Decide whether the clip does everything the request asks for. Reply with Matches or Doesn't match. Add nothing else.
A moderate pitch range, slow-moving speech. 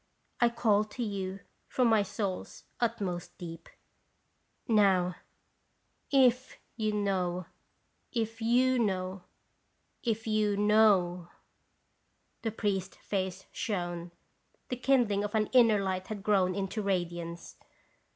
Matches